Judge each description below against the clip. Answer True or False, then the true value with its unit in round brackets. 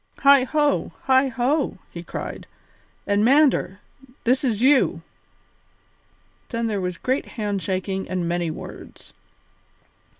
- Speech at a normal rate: False (105 wpm)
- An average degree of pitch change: False (5.8 semitones)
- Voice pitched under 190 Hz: False (230 Hz)